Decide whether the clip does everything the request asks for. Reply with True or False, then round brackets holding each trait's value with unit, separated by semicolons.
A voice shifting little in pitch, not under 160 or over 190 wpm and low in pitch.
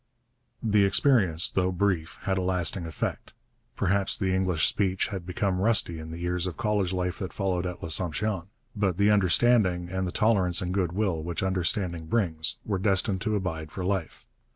True (2.3 semitones; 170 wpm; 95 Hz)